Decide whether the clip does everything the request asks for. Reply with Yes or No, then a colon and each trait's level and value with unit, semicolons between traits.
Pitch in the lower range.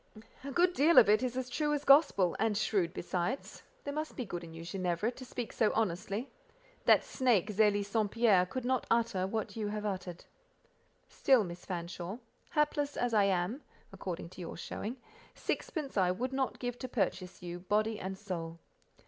No: high, 215 Hz